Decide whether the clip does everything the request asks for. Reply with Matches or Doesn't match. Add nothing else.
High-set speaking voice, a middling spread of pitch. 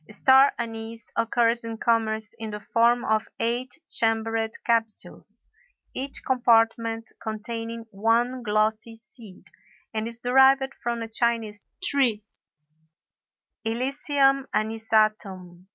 Doesn't match